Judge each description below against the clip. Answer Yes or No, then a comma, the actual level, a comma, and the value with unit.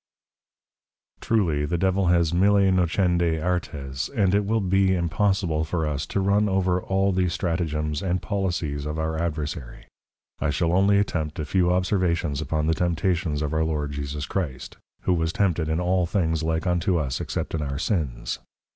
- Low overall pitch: Yes, very low, 85 Hz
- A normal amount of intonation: Yes, average, 3.5 semitones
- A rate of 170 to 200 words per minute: Yes, average, 175 wpm